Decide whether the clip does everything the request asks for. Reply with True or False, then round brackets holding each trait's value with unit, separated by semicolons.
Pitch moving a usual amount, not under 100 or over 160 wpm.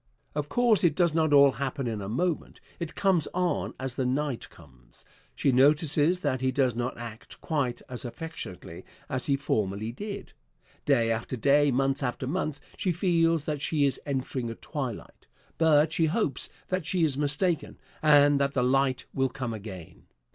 False (4.1 semitones; 175 wpm)